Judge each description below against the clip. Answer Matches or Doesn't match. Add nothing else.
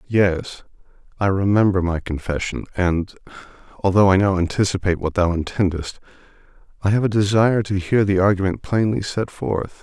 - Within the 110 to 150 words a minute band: Matches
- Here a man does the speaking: Matches